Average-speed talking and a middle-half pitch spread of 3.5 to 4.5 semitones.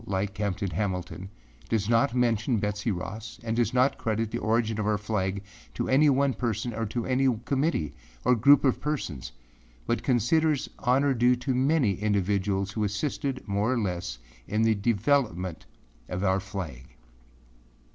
Yes: average, 160 wpm; average, 4.2 semitones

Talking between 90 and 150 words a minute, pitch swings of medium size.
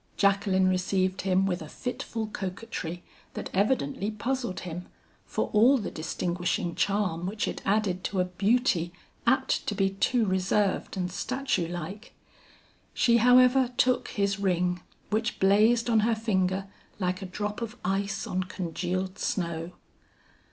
Yes: average, 140 wpm; average, 3.2 semitones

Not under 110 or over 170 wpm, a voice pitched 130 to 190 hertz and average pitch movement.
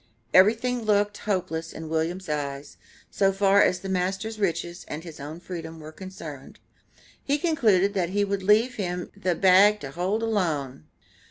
Yes: average, 160 wpm; medium, 185 Hz; average, 4.1 semitones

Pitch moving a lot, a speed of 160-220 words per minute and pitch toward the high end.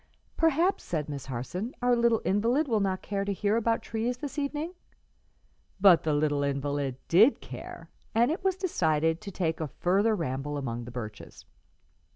Yes: wide, 8.3 semitones; average, 170 wpm; high, 195 Hz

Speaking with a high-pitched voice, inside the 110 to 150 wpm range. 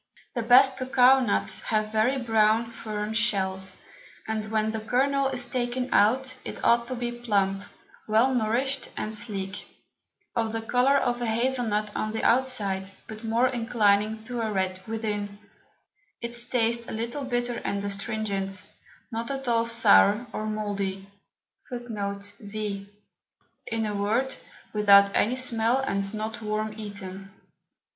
Yes: high, 220 Hz; average, 140 wpm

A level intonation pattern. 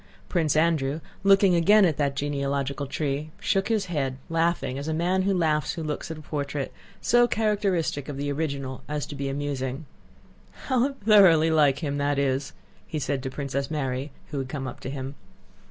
No: average, 3.3 semitones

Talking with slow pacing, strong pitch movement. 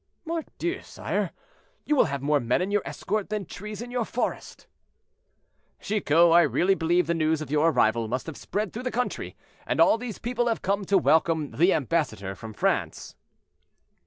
No: average, 180 wpm; wide, 6.1 semitones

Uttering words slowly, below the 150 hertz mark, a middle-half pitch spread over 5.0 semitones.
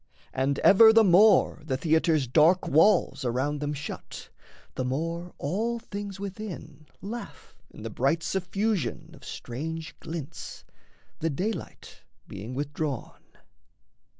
No: slow, 120 wpm; medium, 160 Hz; wide, 5.4 semitones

